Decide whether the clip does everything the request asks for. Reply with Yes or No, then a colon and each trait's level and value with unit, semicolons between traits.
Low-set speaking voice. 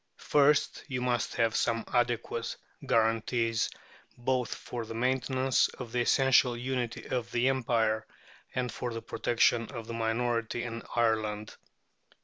Yes: low, 120 Hz